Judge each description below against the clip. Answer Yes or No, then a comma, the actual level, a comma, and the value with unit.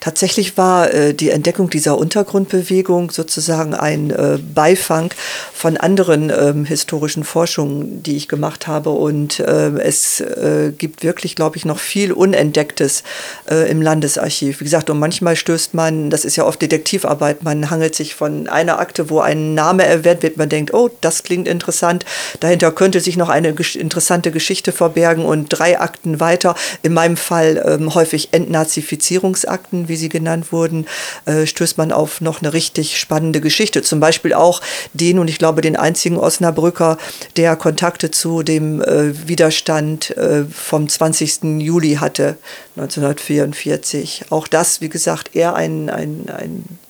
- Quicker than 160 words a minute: No, average, 145 wpm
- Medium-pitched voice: Yes, medium, 160 Hz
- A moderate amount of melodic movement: No, narrow, 2.0 semitones